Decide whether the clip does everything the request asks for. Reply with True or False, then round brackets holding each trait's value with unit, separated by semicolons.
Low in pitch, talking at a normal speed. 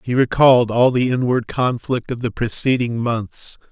True (120 Hz; 160 wpm)